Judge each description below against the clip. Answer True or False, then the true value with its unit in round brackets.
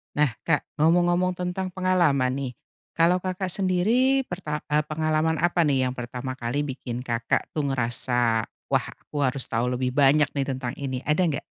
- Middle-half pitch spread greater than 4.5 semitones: True (5.5 semitones)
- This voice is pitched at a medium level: True (150 Hz)